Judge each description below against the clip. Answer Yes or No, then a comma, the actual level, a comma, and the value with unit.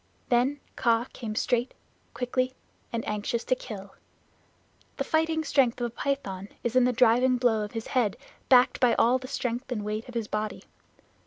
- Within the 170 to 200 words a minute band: Yes, average, 175 wpm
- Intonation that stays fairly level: Yes, narrow, 2.3 semitones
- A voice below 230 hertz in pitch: No, high, 240 Hz